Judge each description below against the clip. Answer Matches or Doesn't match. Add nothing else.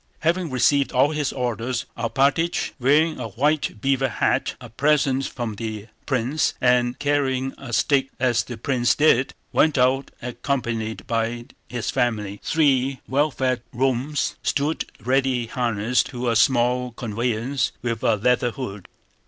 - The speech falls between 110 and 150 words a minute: Matches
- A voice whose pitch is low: Matches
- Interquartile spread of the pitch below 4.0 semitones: Matches